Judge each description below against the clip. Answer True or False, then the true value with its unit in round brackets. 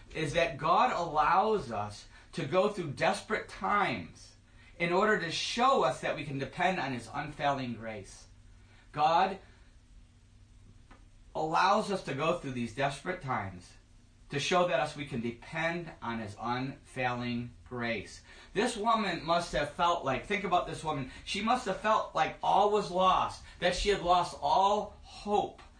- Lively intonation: True (8.0 semitones)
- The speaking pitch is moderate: True (145 Hz)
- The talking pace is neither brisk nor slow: True (155 wpm)